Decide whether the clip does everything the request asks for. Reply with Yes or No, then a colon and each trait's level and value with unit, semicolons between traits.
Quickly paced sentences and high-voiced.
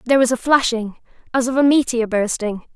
No: average, 195 wpm; high, 245 Hz